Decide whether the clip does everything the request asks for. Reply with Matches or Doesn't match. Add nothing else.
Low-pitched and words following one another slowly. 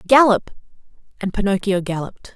Doesn't match